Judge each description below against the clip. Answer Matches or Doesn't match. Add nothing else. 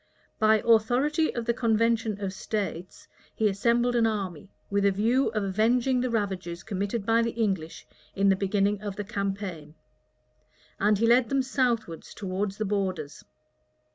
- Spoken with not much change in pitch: Doesn't match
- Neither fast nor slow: Matches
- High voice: Matches